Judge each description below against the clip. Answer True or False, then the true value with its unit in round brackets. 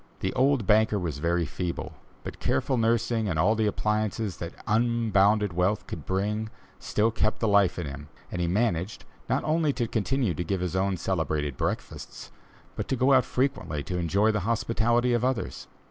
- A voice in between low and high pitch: False (105 Hz)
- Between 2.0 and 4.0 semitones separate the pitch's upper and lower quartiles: False (4.6 semitones)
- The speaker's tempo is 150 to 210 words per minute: True (180 wpm)